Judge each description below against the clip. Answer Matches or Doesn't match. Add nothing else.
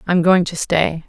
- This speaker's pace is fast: Matches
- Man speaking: Doesn't match